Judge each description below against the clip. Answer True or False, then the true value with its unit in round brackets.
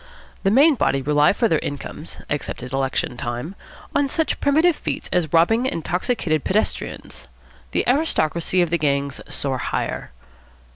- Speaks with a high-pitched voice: False (165 Hz)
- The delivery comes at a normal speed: True (145 wpm)